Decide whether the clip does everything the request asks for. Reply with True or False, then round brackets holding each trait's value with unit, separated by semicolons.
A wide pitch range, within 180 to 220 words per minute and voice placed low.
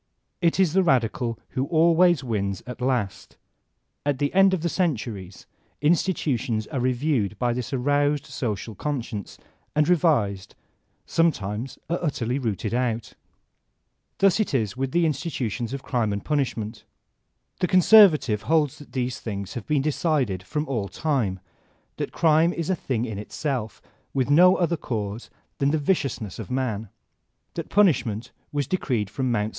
False (5.9 semitones; 155 wpm; 130 Hz)